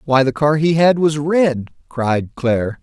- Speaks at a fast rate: No, average, 190 wpm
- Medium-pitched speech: Yes, medium, 145 Hz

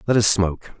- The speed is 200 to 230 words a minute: Yes, fast, 225 wpm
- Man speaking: Yes, male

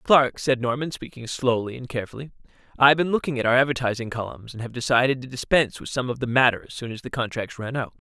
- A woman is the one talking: No, male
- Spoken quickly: Yes, fast, 240 wpm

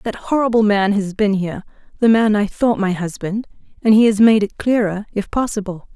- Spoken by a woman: Yes, female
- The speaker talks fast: No, average, 180 wpm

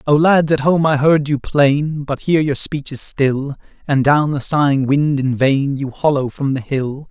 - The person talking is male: Yes, male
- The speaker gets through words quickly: Yes, fast, 220 wpm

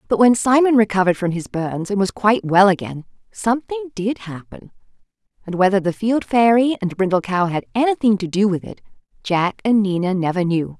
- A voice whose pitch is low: No, high, 205 Hz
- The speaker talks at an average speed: Yes, average, 190 wpm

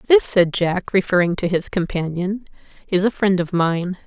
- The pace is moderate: Yes, average, 175 wpm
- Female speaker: Yes, female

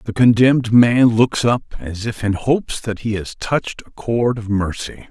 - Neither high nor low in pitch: No, low, 115 Hz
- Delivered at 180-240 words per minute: Yes, average, 200 wpm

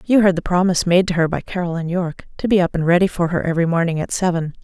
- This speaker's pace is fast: Yes, fast, 270 wpm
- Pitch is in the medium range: Yes, medium, 175 Hz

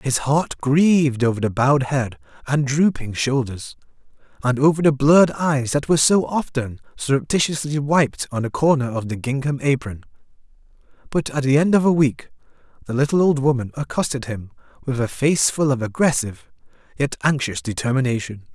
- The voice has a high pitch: No, low, 135 Hz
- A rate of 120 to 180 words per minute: Yes, average, 160 wpm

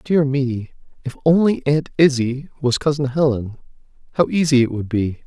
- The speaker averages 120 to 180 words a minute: Yes, average, 150 wpm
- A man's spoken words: Yes, male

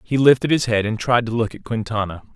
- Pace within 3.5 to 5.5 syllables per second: No, 6.1 syllables/s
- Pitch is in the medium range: No, low, 115 Hz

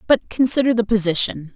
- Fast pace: No, average, 155 wpm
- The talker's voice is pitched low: No, high, 215 Hz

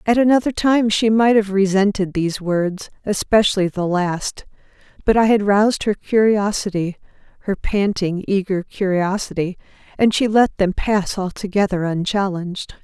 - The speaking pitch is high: Yes, high, 200 Hz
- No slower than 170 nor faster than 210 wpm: No, slow, 135 wpm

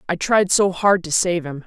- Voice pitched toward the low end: No, medium, 180 Hz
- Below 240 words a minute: No, fast, 250 wpm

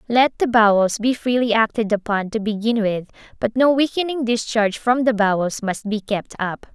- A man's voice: No, female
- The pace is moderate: Yes, average, 185 wpm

